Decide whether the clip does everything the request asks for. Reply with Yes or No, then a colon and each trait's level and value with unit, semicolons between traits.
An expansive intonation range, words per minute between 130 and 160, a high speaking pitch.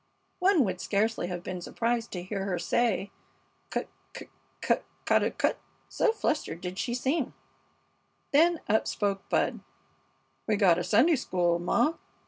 Yes: wide, 6.2 semitones; average, 145 wpm; high, 205 Hz